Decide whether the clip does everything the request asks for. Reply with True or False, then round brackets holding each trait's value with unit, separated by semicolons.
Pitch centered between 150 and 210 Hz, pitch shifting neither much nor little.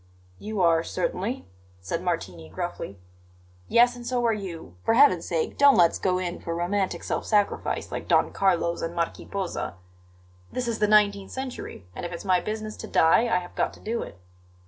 True (190 Hz; 4.4 semitones)